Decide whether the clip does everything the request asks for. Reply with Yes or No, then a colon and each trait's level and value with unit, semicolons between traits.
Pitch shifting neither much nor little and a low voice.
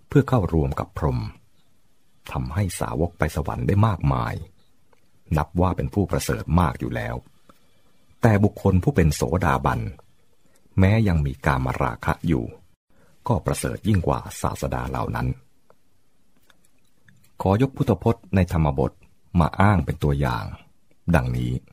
No: wide, 6.9 semitones; very low, 85 Hz